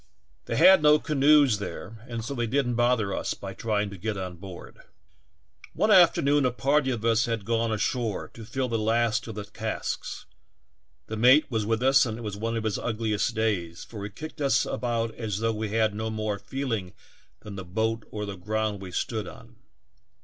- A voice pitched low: Yes, low, 110 Hz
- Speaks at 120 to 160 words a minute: No, average, 200 wpm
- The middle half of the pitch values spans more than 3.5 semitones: No, average, 2.7 semitones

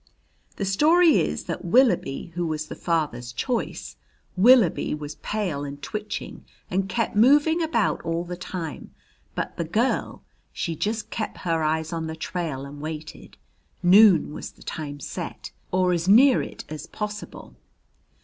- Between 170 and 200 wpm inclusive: No, average, 150 wpm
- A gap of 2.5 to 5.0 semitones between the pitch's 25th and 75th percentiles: No, wide, 5.5 semitones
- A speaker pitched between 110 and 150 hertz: No, medium, 175 Hz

